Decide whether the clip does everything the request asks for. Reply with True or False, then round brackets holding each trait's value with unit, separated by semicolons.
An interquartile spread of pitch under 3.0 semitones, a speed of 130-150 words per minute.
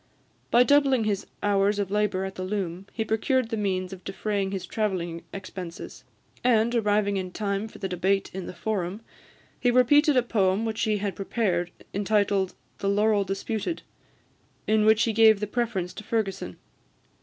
False (2.5 semitones; 165 wpm)